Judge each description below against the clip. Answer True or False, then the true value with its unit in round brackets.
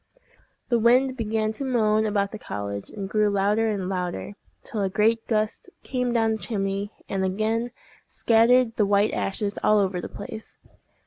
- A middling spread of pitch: False (2.3 semitones)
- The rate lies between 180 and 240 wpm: False (170 wpm)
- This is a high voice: True (215 Hz)